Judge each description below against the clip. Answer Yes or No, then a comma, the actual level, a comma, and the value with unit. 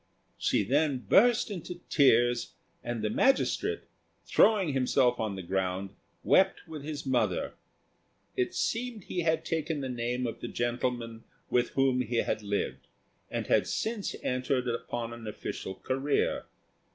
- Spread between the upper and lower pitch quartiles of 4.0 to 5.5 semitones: Yes, average, 5.1 semitones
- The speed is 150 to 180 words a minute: No, average, 140 wpm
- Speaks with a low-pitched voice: Yes, low, 125 Hz